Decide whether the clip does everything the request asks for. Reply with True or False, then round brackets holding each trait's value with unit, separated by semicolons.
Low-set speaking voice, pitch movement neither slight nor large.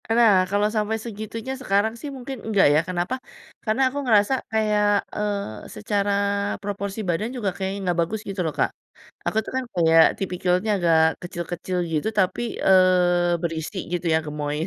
False (195 Hz; 3.7 semitones)